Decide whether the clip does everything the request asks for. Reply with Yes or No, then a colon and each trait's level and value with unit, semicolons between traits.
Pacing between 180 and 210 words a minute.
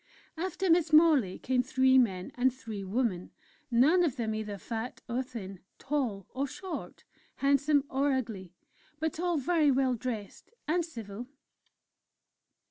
No: slow, 135 wpm